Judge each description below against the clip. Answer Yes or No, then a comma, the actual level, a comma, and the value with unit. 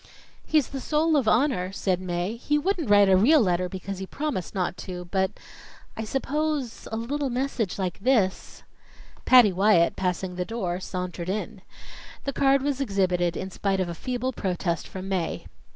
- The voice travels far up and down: Yes, wide, 6.3 semitones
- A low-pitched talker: No, high, 200 Hz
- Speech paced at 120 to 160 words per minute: No, average, 175 wpm